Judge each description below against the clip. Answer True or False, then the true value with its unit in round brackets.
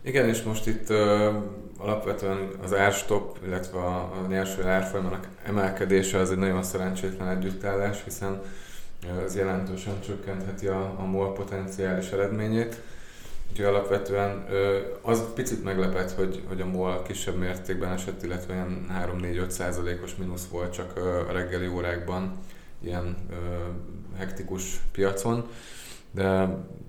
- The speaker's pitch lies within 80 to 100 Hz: True (95 Hz)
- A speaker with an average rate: True (125 wpm)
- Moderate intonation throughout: False (1.4 semitones)